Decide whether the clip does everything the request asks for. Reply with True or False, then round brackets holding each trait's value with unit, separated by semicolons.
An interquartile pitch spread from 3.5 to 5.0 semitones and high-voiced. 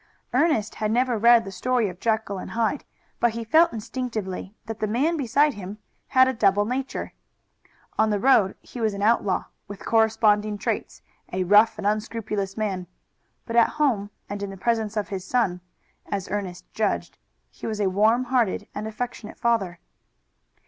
False (2.8 semitones; 215 Hz)